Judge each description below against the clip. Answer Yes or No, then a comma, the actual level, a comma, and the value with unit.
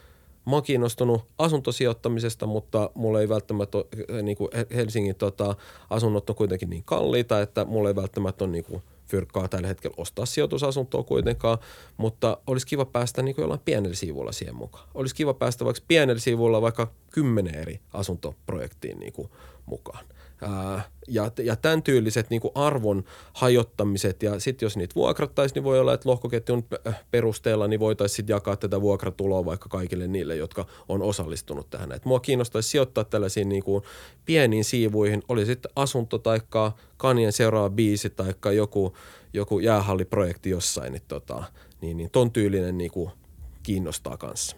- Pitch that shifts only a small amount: No, average, 3.5 semitones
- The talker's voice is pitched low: Yes, low, 105 Hz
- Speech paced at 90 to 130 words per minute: No, average, 150 wpm